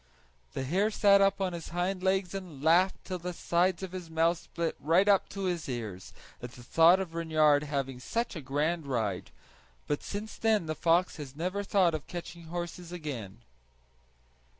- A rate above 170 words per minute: Yes, average, 180 wpm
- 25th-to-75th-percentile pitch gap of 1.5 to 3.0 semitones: No, average, 3.9 semitones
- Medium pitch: Yes, medium, 170 Hz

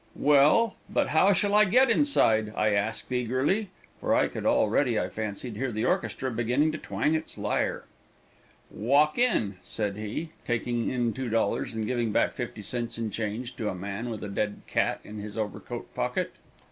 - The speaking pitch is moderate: No, low, 120 Hz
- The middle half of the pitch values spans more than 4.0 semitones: Yes, average, 5.3 semitones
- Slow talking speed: No, average, 175 wpm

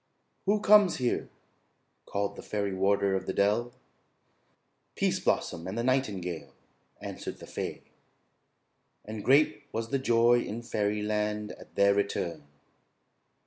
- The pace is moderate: No, slow, 125 wpm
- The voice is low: Yes, low, 105 Hz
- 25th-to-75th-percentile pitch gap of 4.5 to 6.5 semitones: No, average, 3.2 semitones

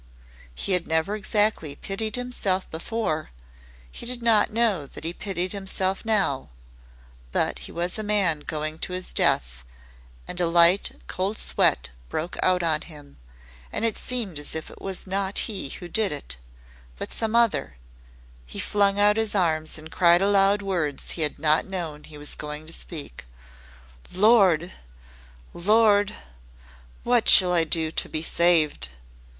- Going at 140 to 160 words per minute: Yes, average, 155 wpm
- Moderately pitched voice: Yes, medium, 180 Hz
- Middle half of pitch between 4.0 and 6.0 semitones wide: Yes, average, 4.7 semitones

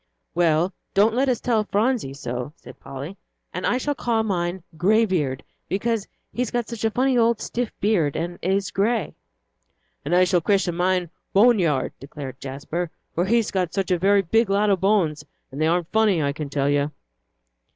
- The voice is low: No, high, 190 Hz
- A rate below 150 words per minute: No, average, 185 wpm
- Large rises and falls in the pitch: Yes, wide, 5.7 semitones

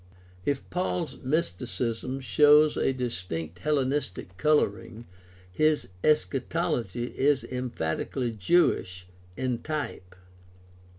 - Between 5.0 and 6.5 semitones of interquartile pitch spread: Yes, wide, 5.5 semitones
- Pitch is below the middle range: Yes, low, 130 Hz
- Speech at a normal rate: No, slow, 80 wpm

